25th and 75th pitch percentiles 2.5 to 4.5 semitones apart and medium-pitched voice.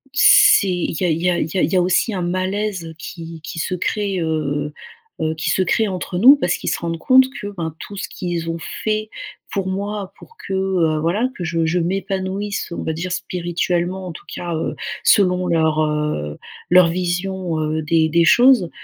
Yes: average, 2.8 semitones; medium, 180 Hz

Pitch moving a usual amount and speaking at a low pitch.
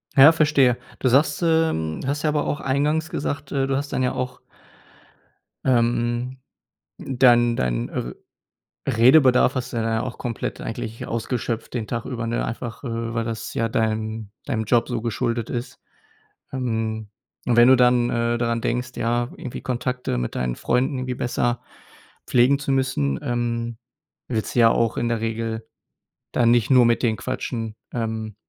No: narrow, 2.1 semitones; low, 120 Hz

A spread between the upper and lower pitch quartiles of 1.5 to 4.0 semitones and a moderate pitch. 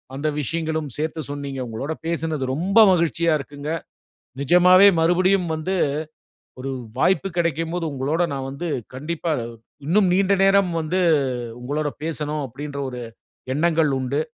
Yes: average, 3.5 semitones; medium, 160 Hz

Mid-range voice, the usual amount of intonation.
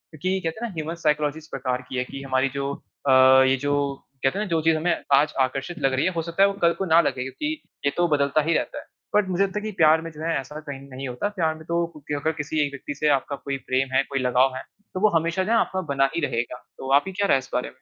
Yes: medium, 150 Hz; average, 3.9 semitones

